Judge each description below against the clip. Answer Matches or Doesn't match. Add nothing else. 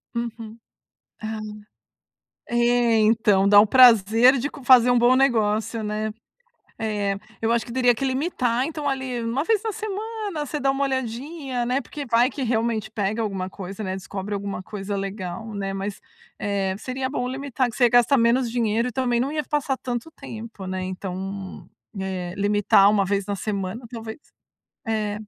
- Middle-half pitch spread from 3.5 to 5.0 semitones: Matches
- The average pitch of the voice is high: Matches